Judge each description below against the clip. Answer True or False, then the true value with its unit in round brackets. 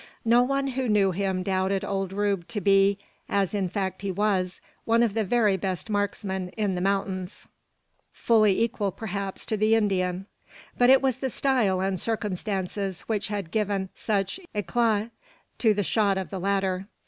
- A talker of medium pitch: False (200 Hz)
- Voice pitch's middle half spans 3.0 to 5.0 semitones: False (2.4 semitones)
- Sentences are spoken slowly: False (170 wpm)